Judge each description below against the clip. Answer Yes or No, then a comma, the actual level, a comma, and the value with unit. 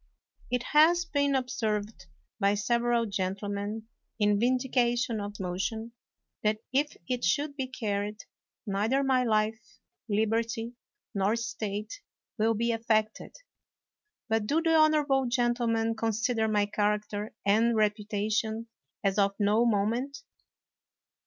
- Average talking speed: No, slow, 120 wpm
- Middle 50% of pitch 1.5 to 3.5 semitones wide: Yes, average, 2.9 semitones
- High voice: Yes, high, 225 Hz